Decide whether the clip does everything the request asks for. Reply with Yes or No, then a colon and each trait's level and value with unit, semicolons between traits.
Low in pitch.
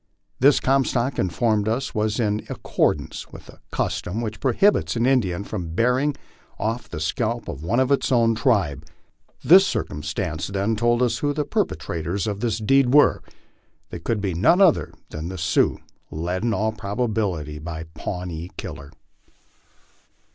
Yes: low, 110 Hz